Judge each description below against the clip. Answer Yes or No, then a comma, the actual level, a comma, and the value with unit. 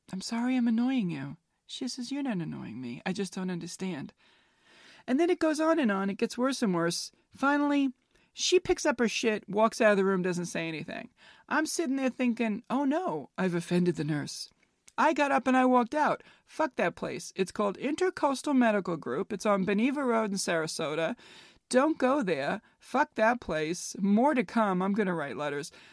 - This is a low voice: No, high, 225 Hz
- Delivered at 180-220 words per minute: Yes, average, 200 wpm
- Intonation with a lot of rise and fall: Yes, wide, 6.3 semitones